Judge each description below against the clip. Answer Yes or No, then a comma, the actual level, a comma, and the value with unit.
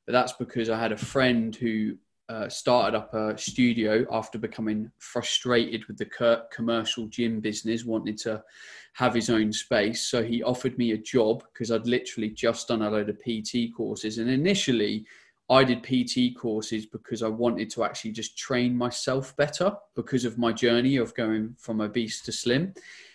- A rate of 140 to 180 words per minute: Yes, average, 175 wpm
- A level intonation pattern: Yes, narrow, 1.9 semitones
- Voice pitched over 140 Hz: No, low, 115 Hz